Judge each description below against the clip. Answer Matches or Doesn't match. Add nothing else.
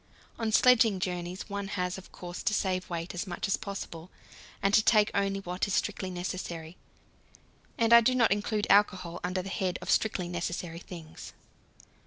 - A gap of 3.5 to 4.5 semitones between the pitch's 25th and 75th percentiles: Doesn't match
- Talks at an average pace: Matches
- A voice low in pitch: Doesn't match